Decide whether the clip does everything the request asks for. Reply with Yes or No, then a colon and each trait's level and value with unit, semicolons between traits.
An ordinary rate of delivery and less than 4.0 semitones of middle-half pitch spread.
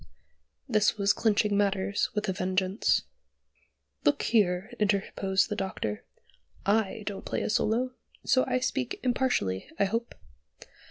No: slow, 125 wpm; average, 2.7 semitones